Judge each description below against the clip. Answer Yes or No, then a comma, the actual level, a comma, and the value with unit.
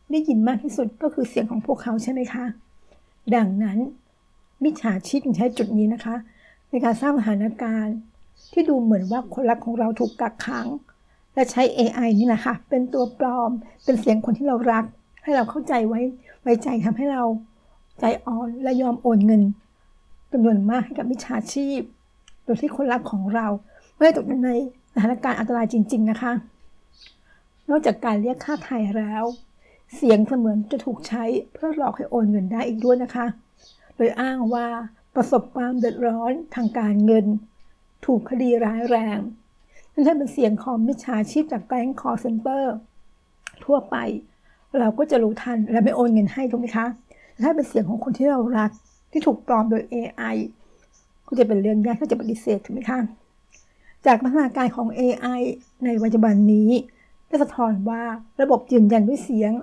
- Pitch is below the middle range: No, high, 240 Hz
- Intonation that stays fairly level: Yes, narrow, 2.3 semitones